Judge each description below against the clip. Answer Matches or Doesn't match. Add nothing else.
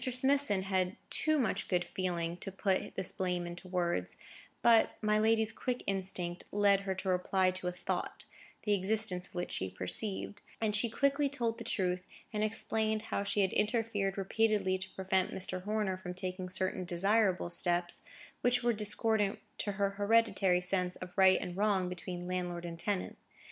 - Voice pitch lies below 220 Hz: Matches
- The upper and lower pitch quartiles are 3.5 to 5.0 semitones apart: Doesn't match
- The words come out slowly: Doesn't match